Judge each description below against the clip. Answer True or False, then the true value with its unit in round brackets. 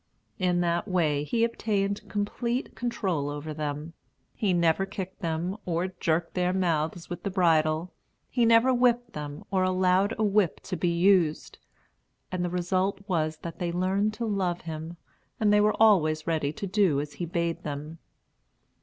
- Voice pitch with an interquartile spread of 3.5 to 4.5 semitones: True (3.8 semitones)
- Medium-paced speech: True (165 wpm)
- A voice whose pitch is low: False (180 Hz)